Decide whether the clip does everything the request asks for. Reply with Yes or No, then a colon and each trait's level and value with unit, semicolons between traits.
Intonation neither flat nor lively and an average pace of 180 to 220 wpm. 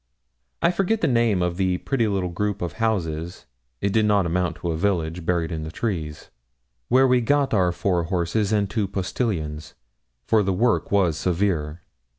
No: average, 4.3 semitones; average, 170 wpm